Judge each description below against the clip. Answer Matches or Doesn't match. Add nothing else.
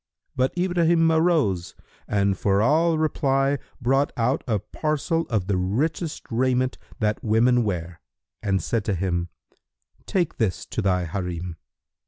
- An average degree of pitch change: Doesn't match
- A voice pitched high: Doesn't match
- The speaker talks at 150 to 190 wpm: Doesn't match